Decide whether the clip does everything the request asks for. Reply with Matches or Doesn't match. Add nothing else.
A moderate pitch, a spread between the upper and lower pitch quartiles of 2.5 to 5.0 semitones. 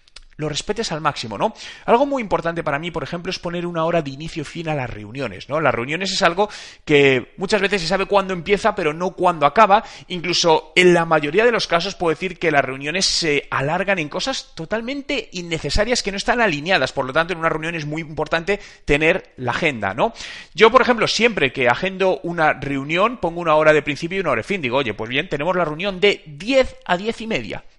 Matches